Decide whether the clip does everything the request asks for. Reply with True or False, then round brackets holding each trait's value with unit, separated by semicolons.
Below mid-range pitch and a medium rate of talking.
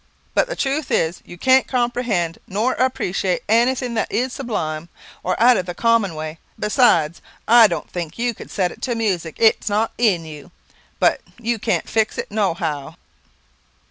False (215 Hz; 175 wpm)